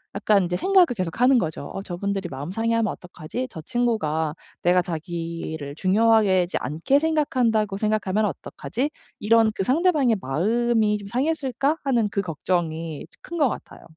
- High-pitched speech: Yes, high, 205 Hz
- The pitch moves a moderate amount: No, wide, 5.7 semitones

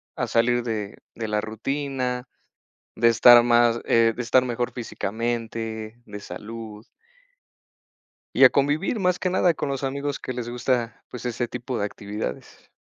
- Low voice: Yes, low, 120 Hz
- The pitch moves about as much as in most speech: No, narrow, 2.2 semitones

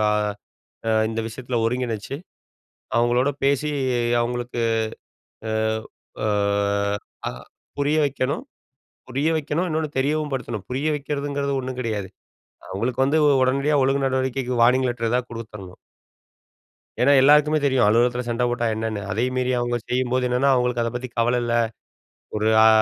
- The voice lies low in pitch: Yes, low, 125 Hz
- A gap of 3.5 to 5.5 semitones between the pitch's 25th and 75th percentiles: No, average, 2.7 semitones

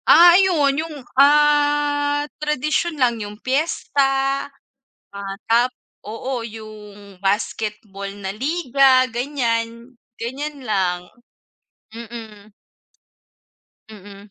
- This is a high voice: Yes, high, 245 Hz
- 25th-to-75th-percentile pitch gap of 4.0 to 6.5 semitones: Yes, wide, 5.4 semitones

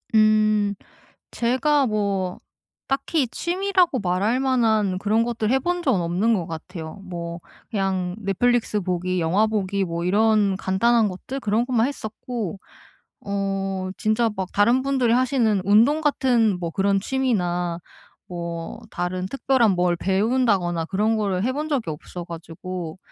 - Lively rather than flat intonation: No, average, 4.7 semitones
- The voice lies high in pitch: Yes, high, 205 Hz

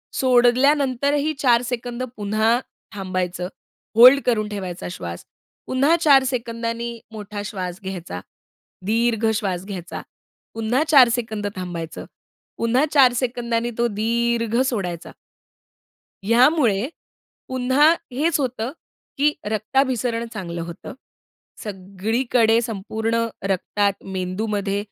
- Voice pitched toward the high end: Yes, high, 230 Hz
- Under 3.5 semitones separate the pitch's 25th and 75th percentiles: No, average, 3.8 semitones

